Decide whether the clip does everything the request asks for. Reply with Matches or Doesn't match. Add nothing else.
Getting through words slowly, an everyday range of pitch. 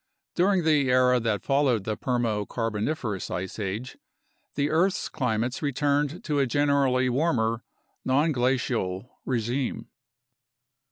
Matches